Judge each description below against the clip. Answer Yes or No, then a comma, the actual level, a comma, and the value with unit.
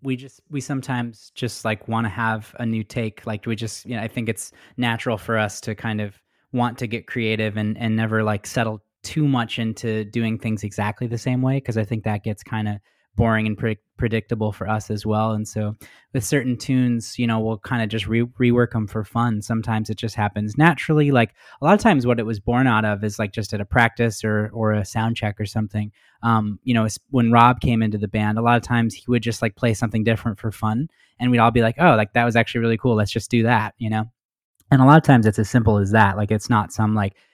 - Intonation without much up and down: Yes, narrow, 1.9 semitones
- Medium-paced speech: No, fast, 255 wpm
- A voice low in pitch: Yes, low, 115 Hz